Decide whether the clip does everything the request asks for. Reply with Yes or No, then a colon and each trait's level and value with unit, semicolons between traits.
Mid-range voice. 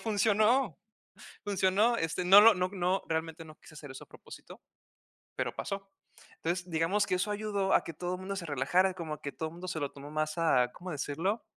Yes: medium, 180 Hz